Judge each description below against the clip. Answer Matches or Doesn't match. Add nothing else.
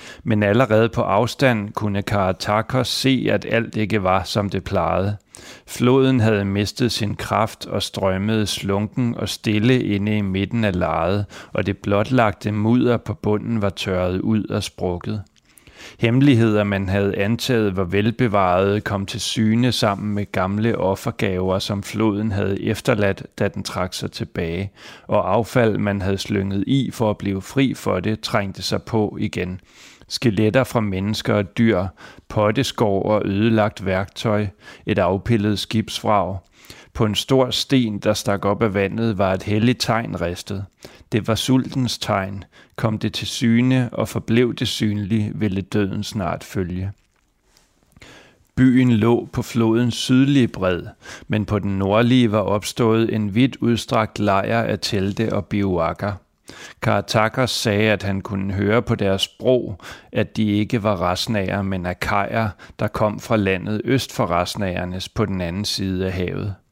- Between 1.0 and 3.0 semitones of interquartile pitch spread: Matches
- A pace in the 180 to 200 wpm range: Doesn't match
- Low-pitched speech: Matches